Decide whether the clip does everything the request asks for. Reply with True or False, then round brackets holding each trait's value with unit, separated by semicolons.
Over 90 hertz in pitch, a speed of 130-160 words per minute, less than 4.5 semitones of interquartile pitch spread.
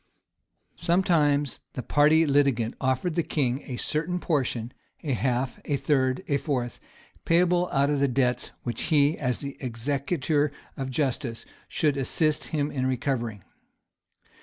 True (140 Hz; 140 wpm; 3.0 semitones)